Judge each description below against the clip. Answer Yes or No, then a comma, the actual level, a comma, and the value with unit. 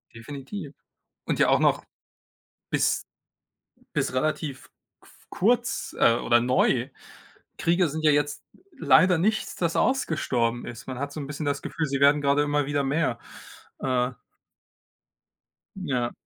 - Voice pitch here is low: No, medium, 145 Hz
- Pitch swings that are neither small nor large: Yes, average, 4.0 semitones